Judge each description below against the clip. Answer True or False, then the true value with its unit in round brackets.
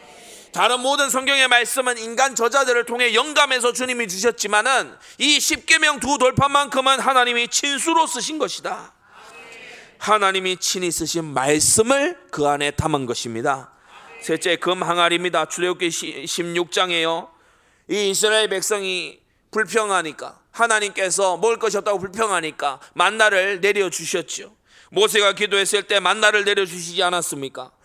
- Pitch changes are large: True (5.9 semitones)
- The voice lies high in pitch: True (205 Hz)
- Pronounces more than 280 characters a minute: True (310 characters per minute)